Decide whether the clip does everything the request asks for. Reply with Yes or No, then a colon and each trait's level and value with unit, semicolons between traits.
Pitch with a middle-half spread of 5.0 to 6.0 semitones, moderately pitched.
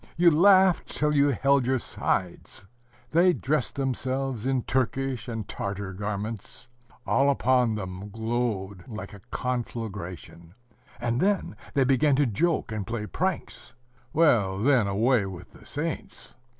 No: average, 5.3 semitones; low, 120 Hz